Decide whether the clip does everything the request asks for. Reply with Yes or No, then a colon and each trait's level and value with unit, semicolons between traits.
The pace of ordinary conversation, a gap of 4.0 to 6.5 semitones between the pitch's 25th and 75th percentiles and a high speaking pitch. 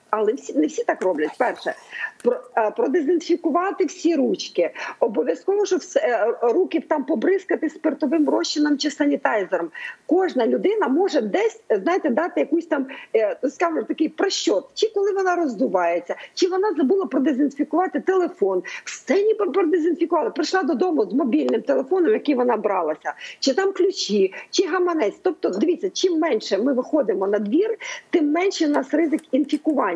Yes: average, 145 wpm; average, 4.9 semitones; very high, 325 Hz